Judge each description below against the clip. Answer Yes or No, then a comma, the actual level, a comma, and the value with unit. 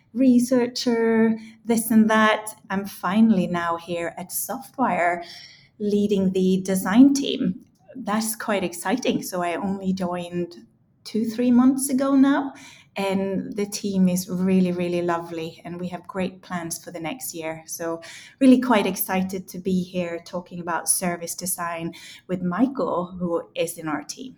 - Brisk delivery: No, average, 150 wpm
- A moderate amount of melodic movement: Yes, average, 4.3 semitones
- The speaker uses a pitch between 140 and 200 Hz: Yes, high, 190 Hz